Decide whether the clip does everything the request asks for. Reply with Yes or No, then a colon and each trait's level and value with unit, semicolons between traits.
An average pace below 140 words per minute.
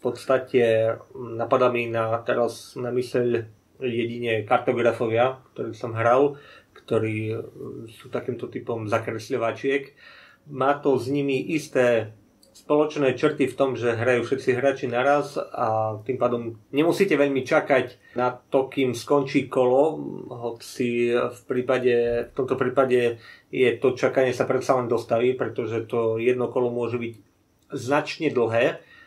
Yes: average, 130 wpm